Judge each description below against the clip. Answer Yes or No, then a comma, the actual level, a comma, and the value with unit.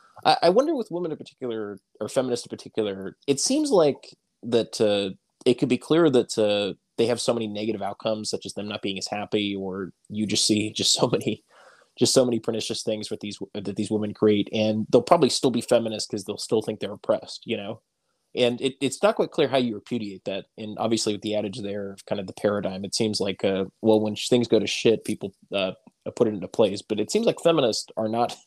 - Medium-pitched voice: No, low, 110 Hz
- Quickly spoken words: Yes, fast, 235 wpm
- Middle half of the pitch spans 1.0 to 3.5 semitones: Yes, narrow, 2.4 semitones